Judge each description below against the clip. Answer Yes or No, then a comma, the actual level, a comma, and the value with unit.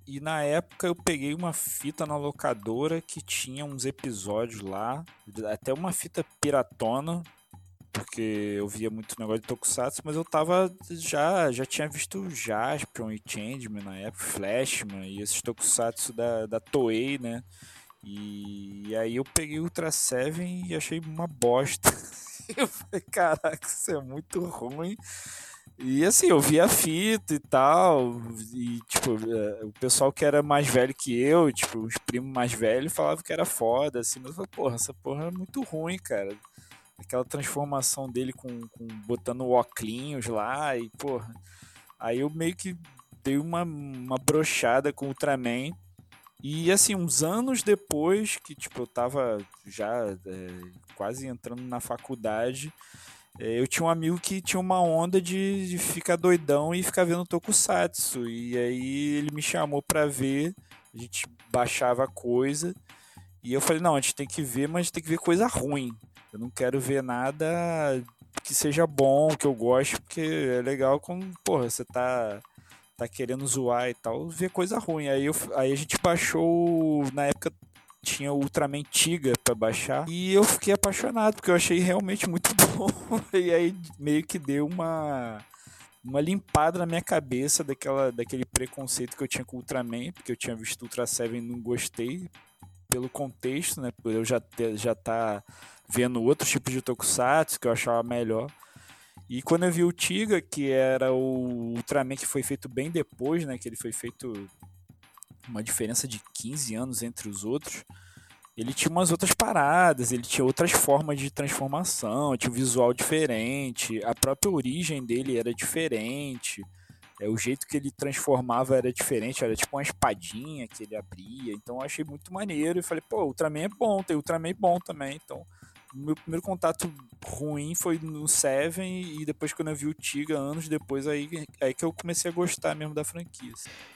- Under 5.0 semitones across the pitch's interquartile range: No, average, 5.3 semitones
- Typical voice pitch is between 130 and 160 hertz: Yes, low, 135 Hz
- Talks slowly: No, average, 175 wpm